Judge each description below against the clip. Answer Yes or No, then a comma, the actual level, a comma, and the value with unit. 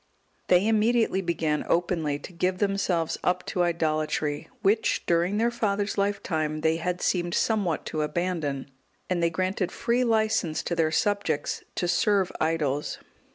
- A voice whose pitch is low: No, medium, 175 Hz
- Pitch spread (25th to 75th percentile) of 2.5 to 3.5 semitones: No, average, 4.0 semitones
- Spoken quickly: No, average, 145 wpm